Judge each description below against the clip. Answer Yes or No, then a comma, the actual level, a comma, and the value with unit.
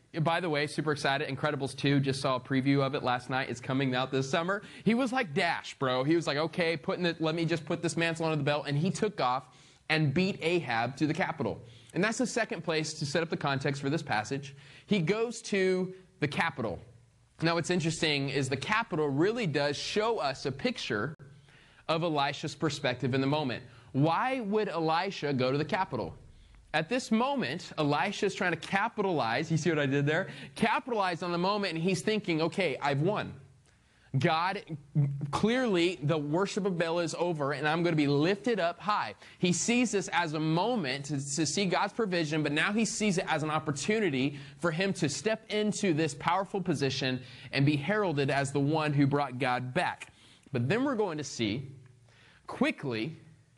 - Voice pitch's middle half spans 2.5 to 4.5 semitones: No, average, 5.0 semitones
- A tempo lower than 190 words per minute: No, average, 200 wpm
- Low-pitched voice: No, medium, 160 Hz